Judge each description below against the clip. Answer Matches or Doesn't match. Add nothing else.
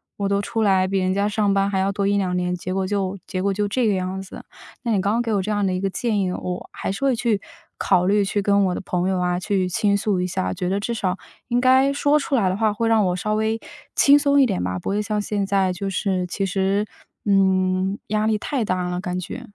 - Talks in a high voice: Matches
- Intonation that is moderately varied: Doesn't match